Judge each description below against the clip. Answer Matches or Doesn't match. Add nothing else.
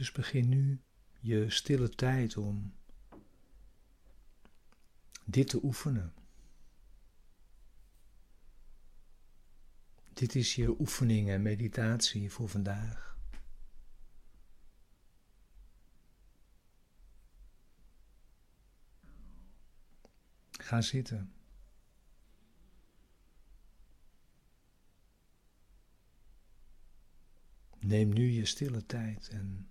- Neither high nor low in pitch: Doesn't match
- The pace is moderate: Doesn't match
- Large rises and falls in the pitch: Doesn't match